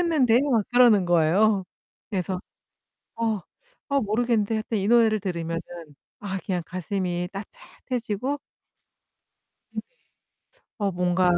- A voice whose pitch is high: Yes, high, 205 Hz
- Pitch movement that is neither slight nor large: Yes, average, 4.1 semitones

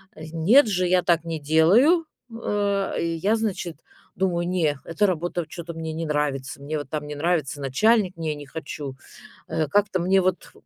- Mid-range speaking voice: Yes, medium, 170 Hz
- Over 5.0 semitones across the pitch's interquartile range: No, average, 3.9 semitones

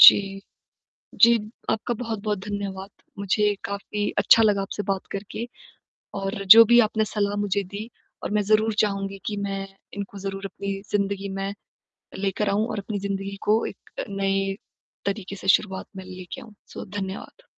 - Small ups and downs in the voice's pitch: Yes, narrow, 1.3 semitones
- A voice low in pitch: No, high, 200 Hz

